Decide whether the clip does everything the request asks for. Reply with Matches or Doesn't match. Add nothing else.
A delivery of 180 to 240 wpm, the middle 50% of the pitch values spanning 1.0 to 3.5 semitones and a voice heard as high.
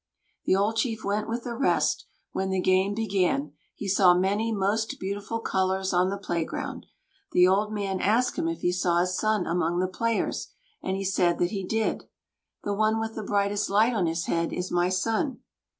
Matches